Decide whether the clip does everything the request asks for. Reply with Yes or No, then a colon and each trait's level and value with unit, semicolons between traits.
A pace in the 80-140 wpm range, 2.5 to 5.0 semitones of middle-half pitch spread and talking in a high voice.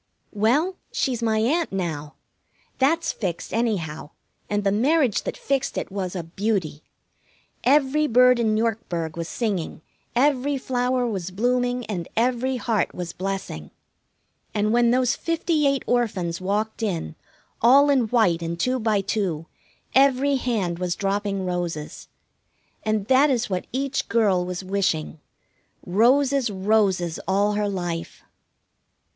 No: slow, 135 wpm; wide, 5.5 semitones; high, 215 Hz